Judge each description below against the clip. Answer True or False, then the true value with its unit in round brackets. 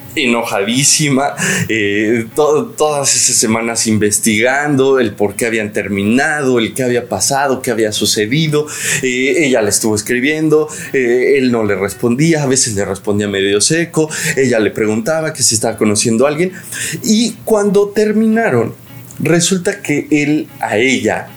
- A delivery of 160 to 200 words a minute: False (145 wpm)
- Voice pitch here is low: True (130 Hz)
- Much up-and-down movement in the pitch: True (6.1 semitones)